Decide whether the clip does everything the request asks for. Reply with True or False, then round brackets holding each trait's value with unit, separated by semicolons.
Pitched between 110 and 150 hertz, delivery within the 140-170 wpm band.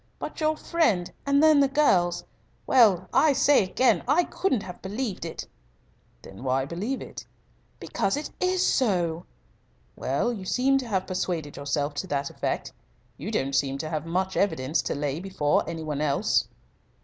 False (185 Hz; 165 wpm)